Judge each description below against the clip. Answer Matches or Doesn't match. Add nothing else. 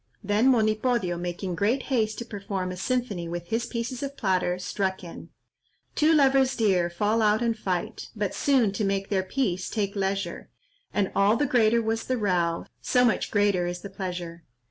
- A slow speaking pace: Doesn't match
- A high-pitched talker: Matches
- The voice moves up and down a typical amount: Matches